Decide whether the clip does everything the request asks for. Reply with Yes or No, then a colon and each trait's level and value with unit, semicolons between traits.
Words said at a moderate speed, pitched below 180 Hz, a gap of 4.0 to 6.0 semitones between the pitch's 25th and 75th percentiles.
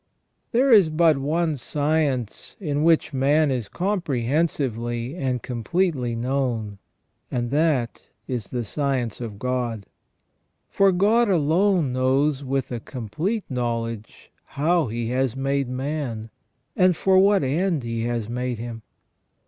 No: slow, 125 wpm; low, 135 Hz; average, 5.1 semitones